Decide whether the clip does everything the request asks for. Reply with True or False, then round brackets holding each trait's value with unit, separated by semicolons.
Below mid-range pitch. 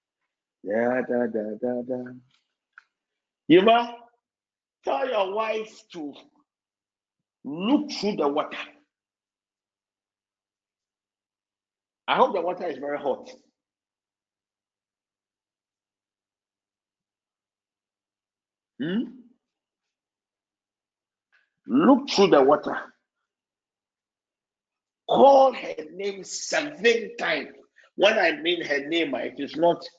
True (115 Hz)